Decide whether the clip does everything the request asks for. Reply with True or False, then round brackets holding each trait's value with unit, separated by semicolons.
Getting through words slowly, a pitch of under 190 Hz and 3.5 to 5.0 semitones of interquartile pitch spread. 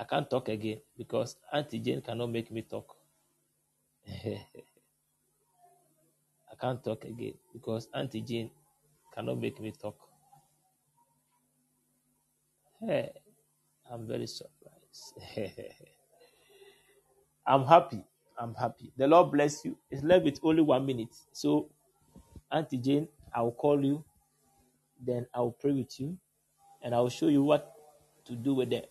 True (125 wpm; 135 Hz; 4.2 semitones)